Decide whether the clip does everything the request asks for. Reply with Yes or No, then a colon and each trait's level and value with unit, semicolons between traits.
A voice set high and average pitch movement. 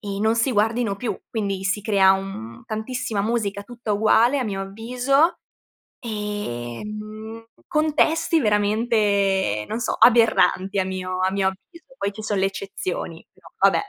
Yes: high, 210 Hz; average, 3.0 semitones